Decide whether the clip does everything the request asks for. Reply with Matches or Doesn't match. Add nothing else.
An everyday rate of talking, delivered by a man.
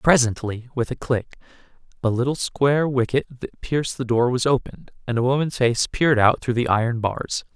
Matches